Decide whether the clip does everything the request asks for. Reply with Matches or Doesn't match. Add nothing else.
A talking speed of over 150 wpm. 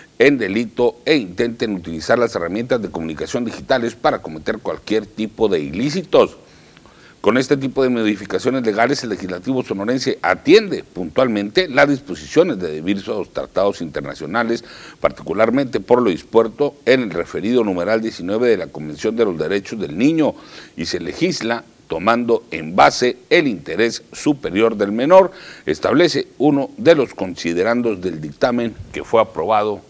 Doesn't match